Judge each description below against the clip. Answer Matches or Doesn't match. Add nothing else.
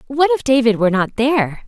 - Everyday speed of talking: Doesn't match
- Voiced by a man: Doesn't match